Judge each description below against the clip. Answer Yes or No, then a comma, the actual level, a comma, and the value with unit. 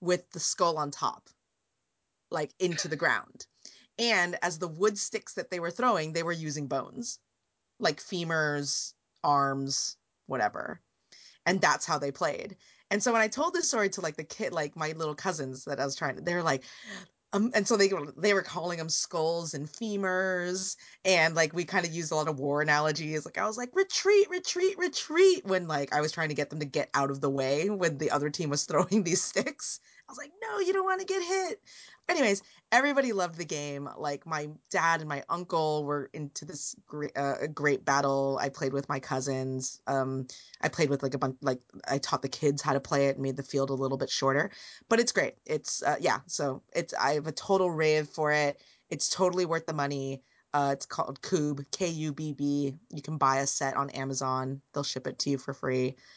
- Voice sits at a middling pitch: Yes, medium, 155 Hz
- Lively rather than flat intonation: No, average, 4.8 semitones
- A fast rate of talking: Yes, fast, 215 wpm